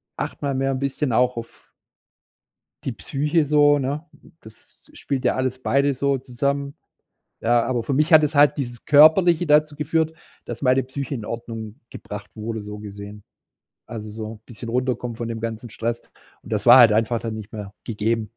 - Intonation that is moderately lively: Yes, average, 3.9 semitones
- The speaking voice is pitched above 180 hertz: No, low, 125 Hz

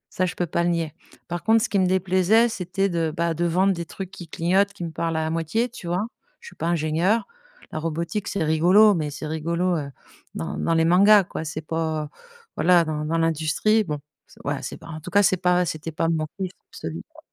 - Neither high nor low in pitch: Yes, medium, 170 Hz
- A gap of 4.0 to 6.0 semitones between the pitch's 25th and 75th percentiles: No, average, 2.9 semitones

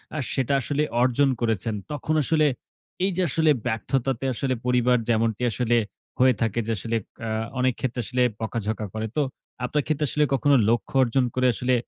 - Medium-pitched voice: No, low, 125 Hz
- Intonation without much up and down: No, average, 3.2 semitones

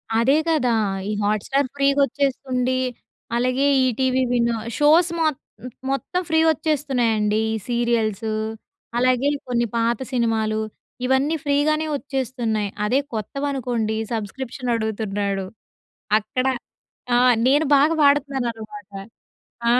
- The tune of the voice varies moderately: Yes, average, 4.0 semitones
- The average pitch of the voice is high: Yes, very high, 250 Hz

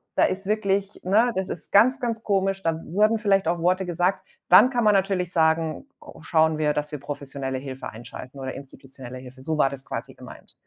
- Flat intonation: No, wide, 5.8 semitones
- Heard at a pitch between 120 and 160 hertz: No, medium, 170 Hz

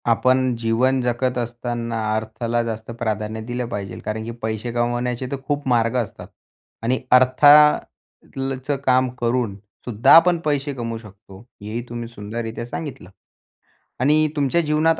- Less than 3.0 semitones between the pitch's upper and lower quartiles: Yes, narrow, 2.5 semitones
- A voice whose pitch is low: Yes, low, 120 Hz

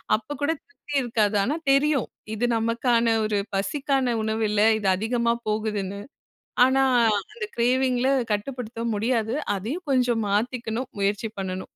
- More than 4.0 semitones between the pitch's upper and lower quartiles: No, average, 3.3 semitones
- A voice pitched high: Yes, high, 230 Hz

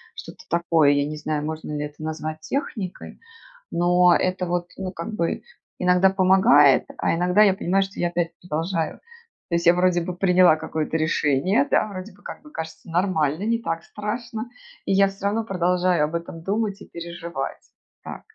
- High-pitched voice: No, medium, 175 Hz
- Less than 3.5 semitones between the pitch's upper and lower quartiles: Yes, average, 3.1 semitones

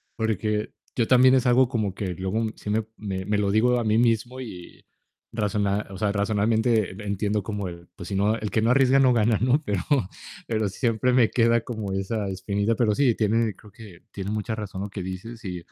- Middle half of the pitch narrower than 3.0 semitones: Yes, narrow, 2.6 semitones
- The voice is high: No, low, 110 Hz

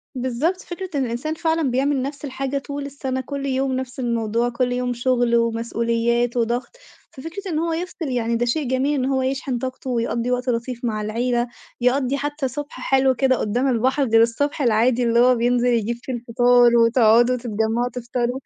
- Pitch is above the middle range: Yes, very high, 250 Hz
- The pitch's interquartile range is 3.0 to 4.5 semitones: No, narrow, 2.4 semitones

